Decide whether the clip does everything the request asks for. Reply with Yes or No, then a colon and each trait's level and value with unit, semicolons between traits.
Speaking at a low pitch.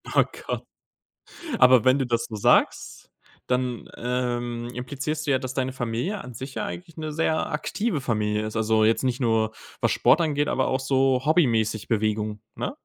Yes: low, 125 Hz